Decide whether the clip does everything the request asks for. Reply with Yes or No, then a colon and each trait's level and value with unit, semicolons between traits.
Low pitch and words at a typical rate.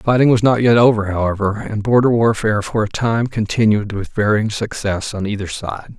Yes: low, 110 Hz; average, 190 wpm